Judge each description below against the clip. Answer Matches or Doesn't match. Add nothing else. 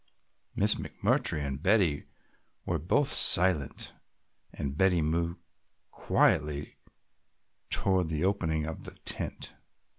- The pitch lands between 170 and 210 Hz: Doesn't match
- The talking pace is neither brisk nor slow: Doesn't match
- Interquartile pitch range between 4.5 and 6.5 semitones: Doesn't match